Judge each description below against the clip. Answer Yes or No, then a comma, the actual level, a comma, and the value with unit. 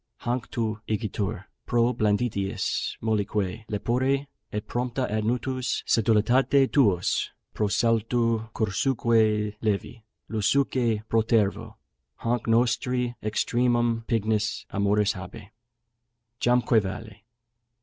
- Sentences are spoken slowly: Yes, slow, 90 wpm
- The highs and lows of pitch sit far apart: No, narrow, 2.4 semitones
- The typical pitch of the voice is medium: No, low, 115 Hz